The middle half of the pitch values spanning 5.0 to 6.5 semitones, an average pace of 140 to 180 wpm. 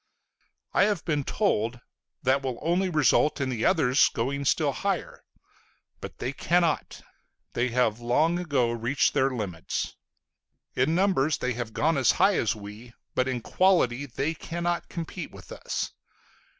Yes: wide, 5.5 semitones; average, 150 wpm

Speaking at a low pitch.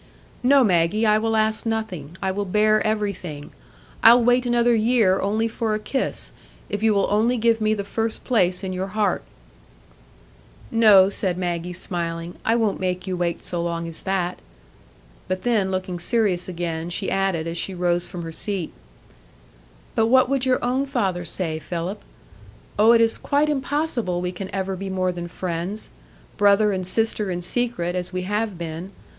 No: high, 195 Hz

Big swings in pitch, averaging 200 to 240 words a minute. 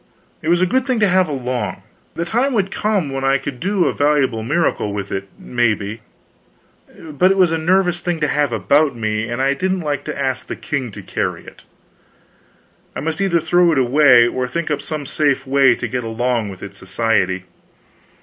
Yes: wide, 6.2 semitones; fast, 205 wpm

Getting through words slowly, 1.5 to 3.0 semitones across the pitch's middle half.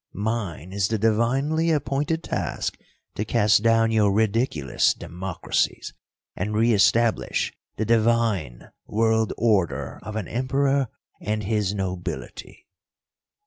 Yes: slow, 110 wpm; average, 2.7 semitones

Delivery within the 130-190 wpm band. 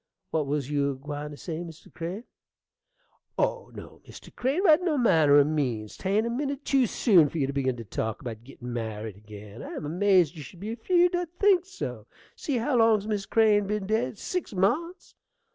No: average, 200 wpm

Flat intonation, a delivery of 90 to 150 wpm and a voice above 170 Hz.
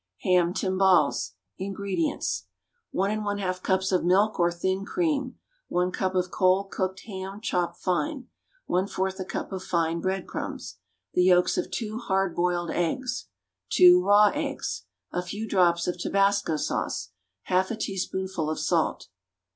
Yes: narrow, 2.1 semitones; average, 145 wpm; high, 190 Hz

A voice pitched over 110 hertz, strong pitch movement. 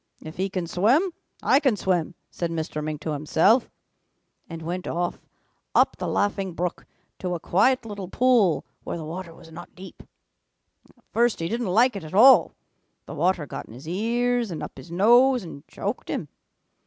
Yes: medium, 185 Hz; wide, 5.7 semitones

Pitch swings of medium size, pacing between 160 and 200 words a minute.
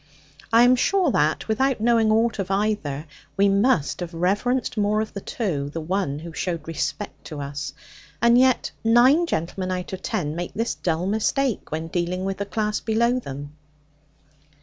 No: wide, 5.8 semitones; average, 170 wpm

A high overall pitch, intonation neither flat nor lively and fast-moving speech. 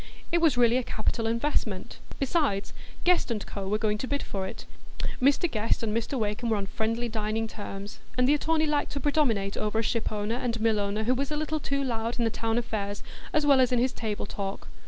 Yes: high, 230 Hz; average, 4.5 semitones; fast, 220 wpm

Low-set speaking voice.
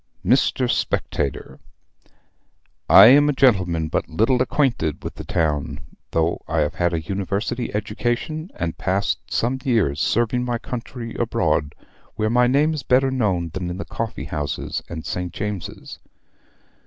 Yes: low, 105 Hz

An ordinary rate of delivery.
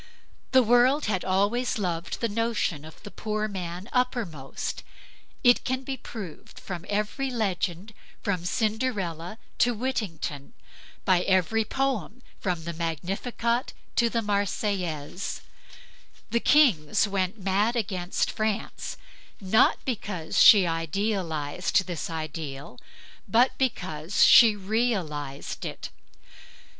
No: slow, 110 wpm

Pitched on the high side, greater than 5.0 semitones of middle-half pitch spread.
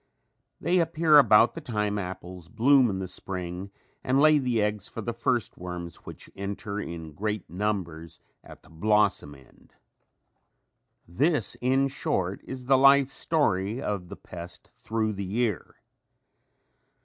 No: low, 105 Hz; wide, 5.6 semitones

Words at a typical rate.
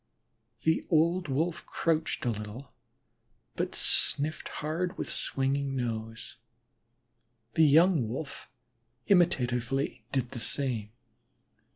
No: slow, 95 wpm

